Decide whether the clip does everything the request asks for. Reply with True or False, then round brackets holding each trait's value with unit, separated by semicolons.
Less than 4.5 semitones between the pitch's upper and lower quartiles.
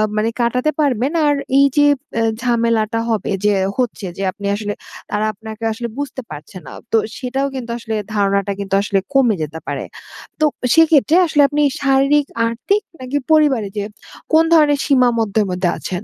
False (5.2 semitones)